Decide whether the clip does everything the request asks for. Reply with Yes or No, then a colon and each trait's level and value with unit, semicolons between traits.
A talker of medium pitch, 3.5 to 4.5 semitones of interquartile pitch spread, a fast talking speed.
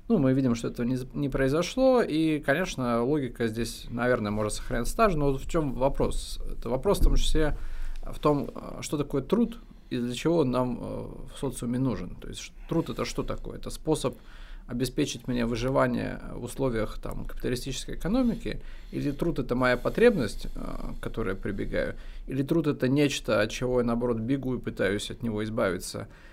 No: low, 130 Hz; average, 4.0 semitones; fast, 175 wpm